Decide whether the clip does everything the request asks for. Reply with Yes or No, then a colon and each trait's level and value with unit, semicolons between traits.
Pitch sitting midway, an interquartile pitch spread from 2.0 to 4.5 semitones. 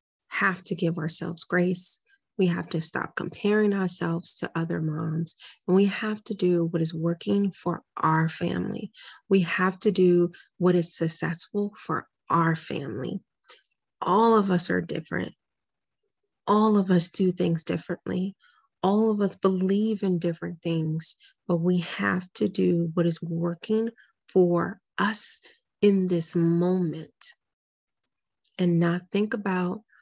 Yes: medium, 180 Hz; average, 3.1 semitones